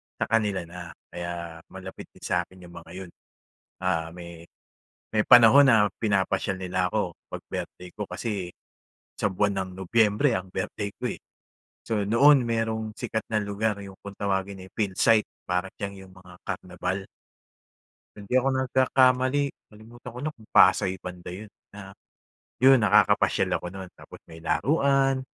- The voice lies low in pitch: Yes, low, 100 Hz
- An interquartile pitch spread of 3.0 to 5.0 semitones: Yes, average, 3.7 semitones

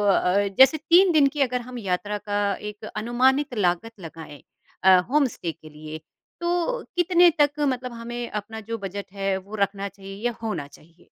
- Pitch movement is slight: No, average, 5.1 semitones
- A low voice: No, high, 210 Hz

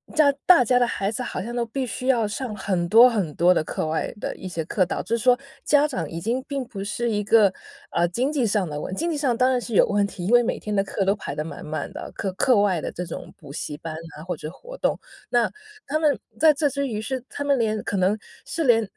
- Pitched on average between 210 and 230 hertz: Yes, high, 220 Hz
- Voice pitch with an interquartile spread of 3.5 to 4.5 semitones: No, wide, 5.6 semitones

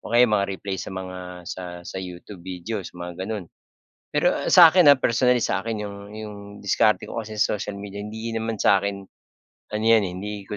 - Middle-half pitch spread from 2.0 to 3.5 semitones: Yes, average, 2.7 semitones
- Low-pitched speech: Yes, low, 105 Hz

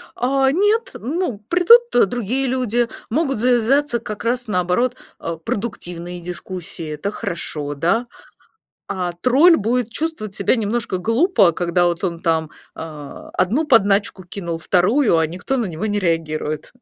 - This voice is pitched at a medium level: No, high, 210 Hz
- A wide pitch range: Yes, wide, 6.5 semitones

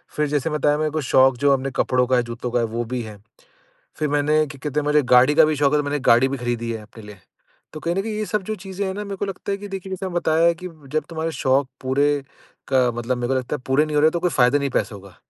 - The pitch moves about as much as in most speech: Yes, average, 4.1 semitones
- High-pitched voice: No, medium, 145 Hz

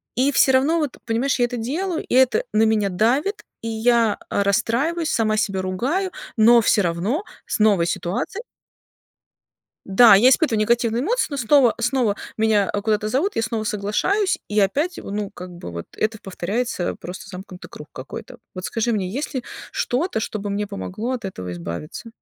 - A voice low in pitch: No, high, 225 Hz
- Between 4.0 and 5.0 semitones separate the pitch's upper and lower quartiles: Yes, average, 4.6 semitones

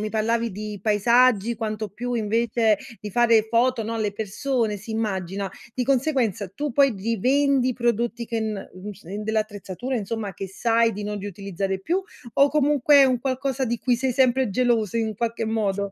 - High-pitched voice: Yes, high, 225 Hz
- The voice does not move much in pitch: No, average, 3.1 semitones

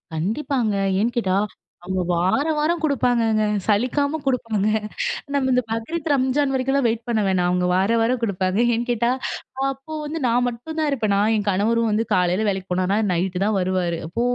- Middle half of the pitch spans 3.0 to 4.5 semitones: No, wide, 5.4 semitones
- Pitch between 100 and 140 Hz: No, high, 225 Hz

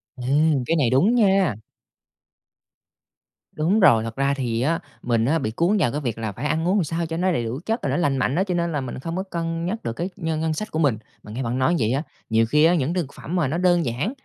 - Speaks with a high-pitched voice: No, medium, 155 Hz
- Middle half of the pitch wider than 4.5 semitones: Yes, wide, 5.4 semitones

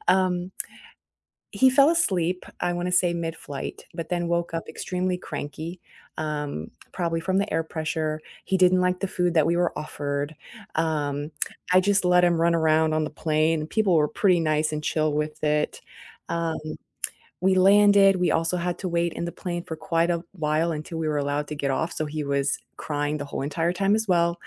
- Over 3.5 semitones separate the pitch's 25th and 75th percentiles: No, average, 2.8 semitones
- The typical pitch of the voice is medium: Yes, medium, 165 Hz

